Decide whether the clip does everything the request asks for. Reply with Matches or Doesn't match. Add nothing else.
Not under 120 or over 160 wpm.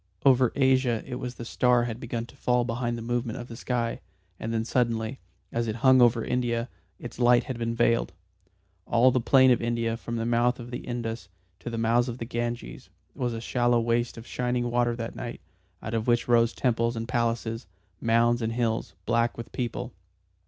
Doesn't match